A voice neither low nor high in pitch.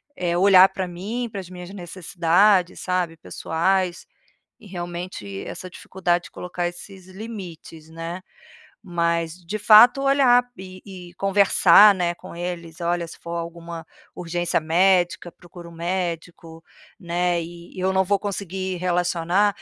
Yes: medium, 180 Hz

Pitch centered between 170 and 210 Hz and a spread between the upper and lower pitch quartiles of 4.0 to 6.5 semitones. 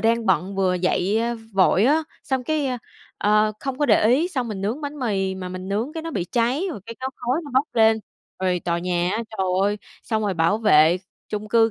No: high, 220 Hz; average, 5.1 semitones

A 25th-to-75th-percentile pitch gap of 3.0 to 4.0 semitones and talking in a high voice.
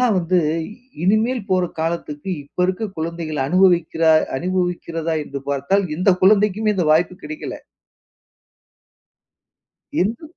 No: average, 3.6 semitones; medium, 180 Hz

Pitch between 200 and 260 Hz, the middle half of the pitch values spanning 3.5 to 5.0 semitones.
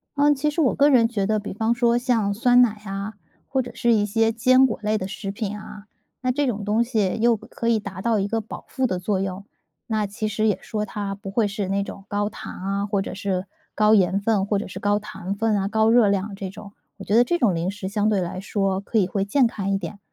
No: high, 210 Hz; narrow, 2.5 semitones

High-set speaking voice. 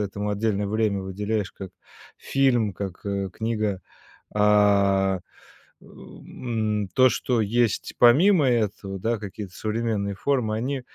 No: low, 105 Hz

